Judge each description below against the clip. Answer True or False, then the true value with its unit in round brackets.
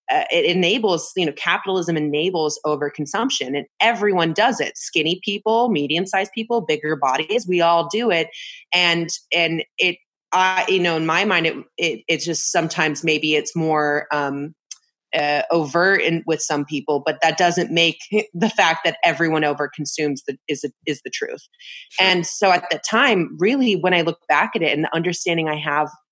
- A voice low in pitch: False (170 Hz)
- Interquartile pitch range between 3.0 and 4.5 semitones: True (3.9 semitones)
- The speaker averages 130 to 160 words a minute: False (180 wpm)